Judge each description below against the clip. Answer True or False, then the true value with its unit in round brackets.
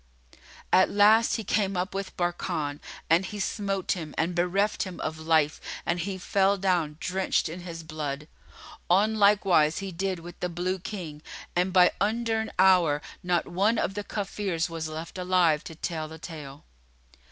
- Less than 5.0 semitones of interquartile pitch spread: True (3.3 semitones)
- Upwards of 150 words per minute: True (165 wpm)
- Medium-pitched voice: True (180 Hz)